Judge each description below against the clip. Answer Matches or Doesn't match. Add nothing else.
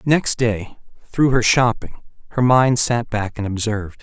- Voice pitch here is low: Matches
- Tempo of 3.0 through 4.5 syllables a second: Matches